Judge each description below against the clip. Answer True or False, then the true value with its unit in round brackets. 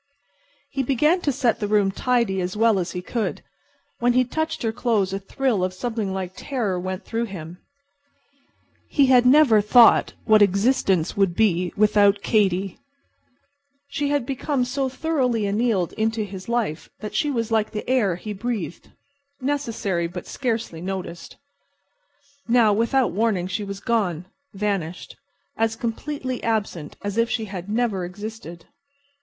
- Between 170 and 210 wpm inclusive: False (150 wpm)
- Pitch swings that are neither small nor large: True (4.3 semitones)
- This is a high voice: True (215 Hz)